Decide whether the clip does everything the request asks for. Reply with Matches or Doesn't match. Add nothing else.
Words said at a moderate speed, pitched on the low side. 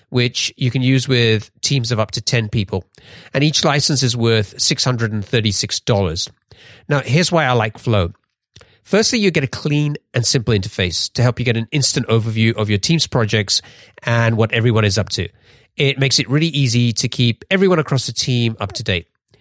Matches